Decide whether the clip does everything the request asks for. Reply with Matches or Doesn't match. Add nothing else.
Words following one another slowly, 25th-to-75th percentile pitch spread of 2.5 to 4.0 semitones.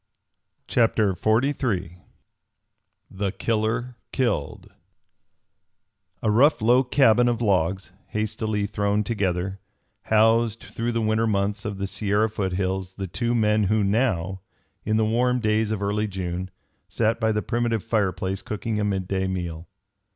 Matches